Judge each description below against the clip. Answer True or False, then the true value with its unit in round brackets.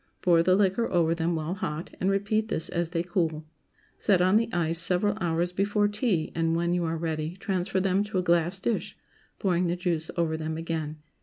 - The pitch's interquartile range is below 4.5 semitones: True (2.7 semitones)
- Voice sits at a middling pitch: True (175 Hz)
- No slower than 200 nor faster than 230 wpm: True (205 wpm)